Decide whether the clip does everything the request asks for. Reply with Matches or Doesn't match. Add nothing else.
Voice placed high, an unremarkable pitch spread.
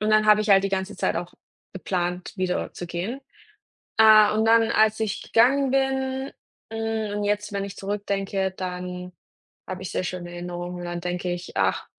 Matches